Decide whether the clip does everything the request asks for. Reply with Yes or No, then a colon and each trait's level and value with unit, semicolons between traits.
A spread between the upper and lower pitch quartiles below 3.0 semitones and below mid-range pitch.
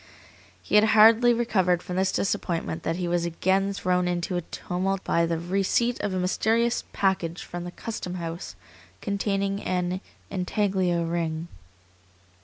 No: narrow, 2.4 semitones; medium, 185 Hz